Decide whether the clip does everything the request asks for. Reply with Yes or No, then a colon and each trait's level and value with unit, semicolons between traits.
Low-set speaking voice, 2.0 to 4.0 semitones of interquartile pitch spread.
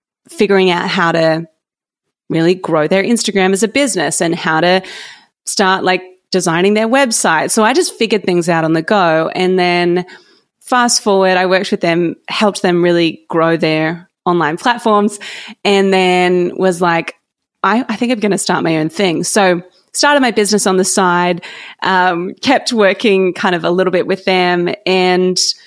No: medium, 185 Hz; average, 3.0 semitones